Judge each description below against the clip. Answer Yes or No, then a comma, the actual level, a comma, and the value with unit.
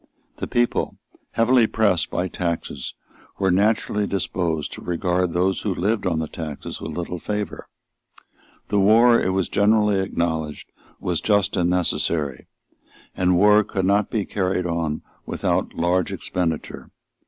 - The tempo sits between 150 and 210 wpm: No, average, 140 wpm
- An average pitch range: Yes, average, 3.2 semitones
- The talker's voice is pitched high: No, very low, 90 Hz